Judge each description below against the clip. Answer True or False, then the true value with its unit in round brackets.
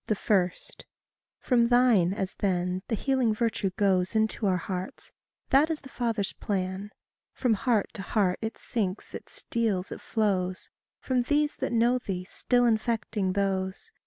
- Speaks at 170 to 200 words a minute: False (150 wpm)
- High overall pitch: True (215 Hz)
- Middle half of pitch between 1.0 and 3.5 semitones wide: False (4.1 semitones)